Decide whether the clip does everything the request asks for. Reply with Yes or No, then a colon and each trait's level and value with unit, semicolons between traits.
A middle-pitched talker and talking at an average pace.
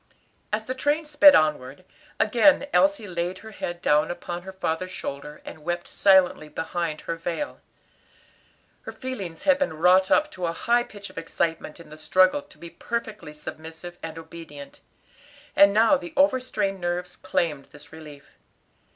Yes: medium, 180 Hz; average, 160 wpm